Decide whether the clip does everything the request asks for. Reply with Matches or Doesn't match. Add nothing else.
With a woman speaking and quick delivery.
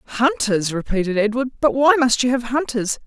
Doesn't match